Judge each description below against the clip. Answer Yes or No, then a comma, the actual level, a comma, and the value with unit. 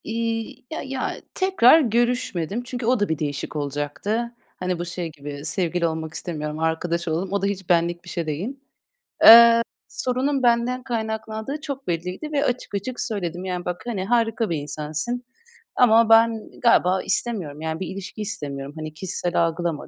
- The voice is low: No, high, 190 Hz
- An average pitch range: No, wide, 6.3 semitones